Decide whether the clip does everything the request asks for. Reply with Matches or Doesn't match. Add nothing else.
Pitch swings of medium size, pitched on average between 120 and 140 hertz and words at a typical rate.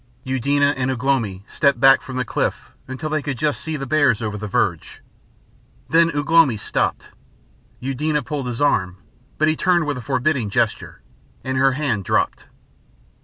Matches